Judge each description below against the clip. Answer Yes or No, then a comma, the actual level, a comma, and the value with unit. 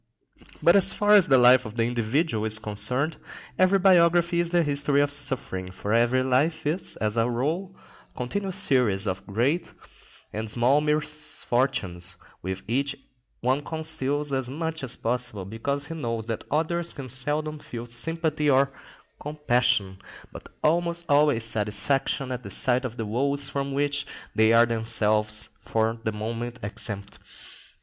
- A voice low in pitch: Yes, low, 130 Hz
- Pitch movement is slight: No, average, 5.0 semitones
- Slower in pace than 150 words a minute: No, average, 155 wpm